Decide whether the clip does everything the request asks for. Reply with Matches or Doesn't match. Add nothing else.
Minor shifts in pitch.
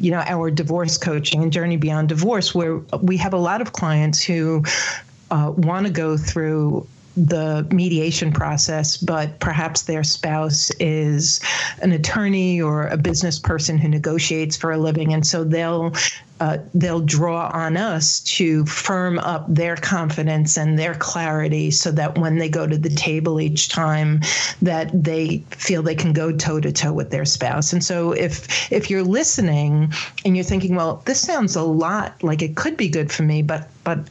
Matches